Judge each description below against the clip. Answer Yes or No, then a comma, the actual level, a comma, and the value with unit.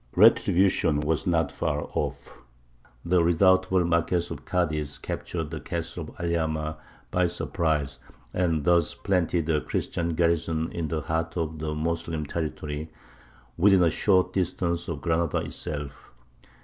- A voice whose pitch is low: Yes, very low, 85 Hz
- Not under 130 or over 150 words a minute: Yes, slow, 135 wpm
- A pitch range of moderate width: No, narrow, 2.1 semitones